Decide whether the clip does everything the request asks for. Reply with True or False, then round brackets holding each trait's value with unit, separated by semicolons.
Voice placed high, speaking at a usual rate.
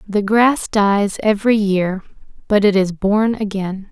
True (205 Hz; 155 wpm)